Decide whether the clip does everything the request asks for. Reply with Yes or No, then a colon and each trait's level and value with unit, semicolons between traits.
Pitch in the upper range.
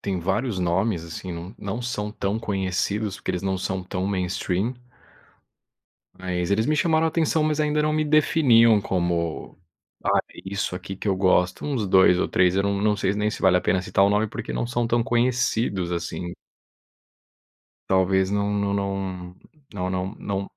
No: low, 100 Hz